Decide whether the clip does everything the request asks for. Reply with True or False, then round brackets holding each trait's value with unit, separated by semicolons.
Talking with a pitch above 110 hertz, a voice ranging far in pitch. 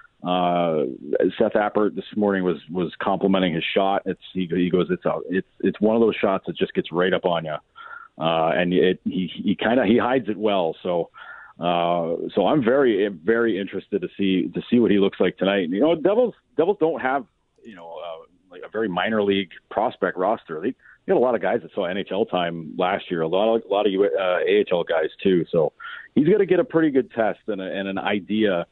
False (100 Hz; 6.3 semitones)